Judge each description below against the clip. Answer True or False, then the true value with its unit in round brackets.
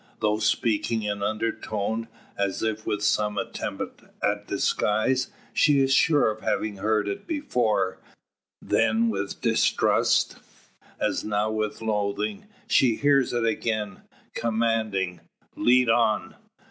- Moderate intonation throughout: False (2.1 semitones)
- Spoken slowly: True (120 wpm)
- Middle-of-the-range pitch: False (110 Hz)